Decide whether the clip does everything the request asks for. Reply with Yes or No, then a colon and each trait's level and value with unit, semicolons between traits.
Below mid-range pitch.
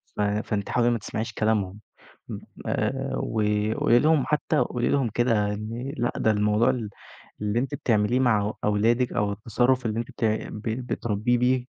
Yes: low, 110 Hz